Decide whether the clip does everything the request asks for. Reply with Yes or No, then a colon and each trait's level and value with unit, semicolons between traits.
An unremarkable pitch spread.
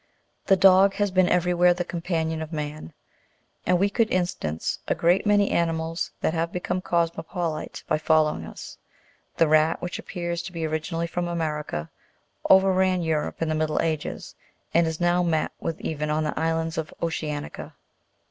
No: narrow, 2.2 semitones